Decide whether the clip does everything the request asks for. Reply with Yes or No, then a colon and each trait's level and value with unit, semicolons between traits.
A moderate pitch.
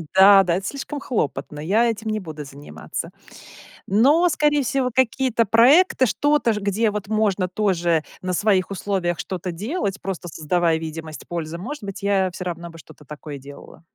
No: high, 195 Hz